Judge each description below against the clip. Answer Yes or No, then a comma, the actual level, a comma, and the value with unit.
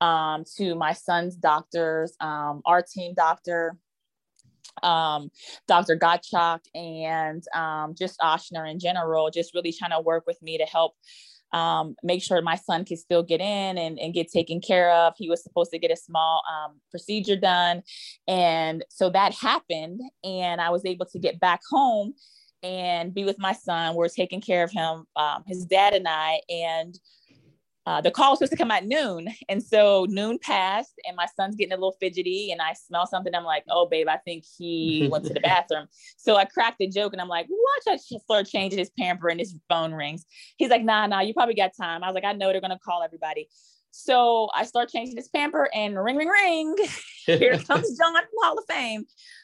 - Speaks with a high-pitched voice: No, medium, 180 Hz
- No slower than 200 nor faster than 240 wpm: Yes, fast, 205 wpm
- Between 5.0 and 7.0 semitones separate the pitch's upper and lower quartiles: No, average, 3.9 semitones